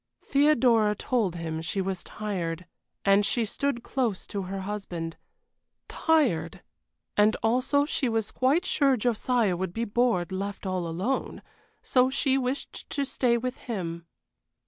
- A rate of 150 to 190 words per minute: No, average, 140 wpm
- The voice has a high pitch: Yes, high, 215 Hz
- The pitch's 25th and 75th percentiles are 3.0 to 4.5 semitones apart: No, wide, 5.4 semitones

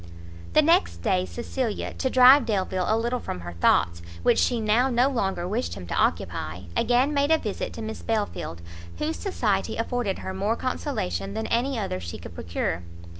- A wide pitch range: Yes, wide, 6.7 semitones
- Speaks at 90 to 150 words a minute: No, average, 180 wpm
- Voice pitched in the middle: No, high, 220 Hz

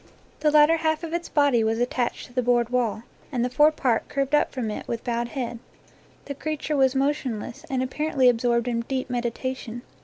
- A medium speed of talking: No, fast, 210 wpm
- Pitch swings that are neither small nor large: Yes, average, 3.5 semitones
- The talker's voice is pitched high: Yes, very high, 255 Hz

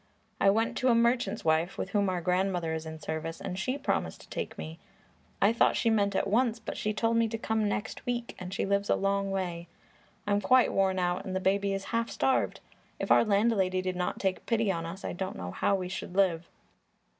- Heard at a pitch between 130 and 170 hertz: No, high, 195 Hz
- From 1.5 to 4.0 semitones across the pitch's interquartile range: Yes, average, 3.5 semitones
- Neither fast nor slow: No, fast, 225 wpm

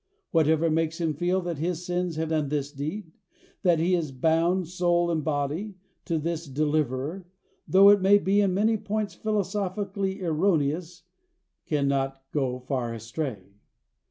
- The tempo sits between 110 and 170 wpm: Yes, average, 145 wpm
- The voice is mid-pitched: Yes, medium, 165 Hz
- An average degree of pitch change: Yes, average, 4.0 semitones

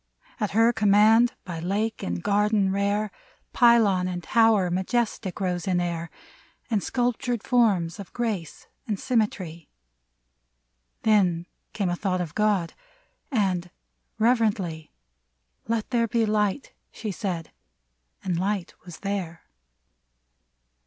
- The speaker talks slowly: Yes, slow, 125 wpm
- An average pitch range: Yes, average, 3.9 semitones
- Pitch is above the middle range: Yes, high, 200 Hz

